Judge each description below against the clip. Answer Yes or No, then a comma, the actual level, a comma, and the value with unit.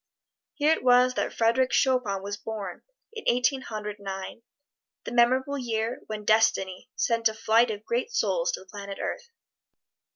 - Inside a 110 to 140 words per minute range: No, average, 160 wpm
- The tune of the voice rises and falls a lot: No, average, 3.4 semitones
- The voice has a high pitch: Yes, high, 230 Hz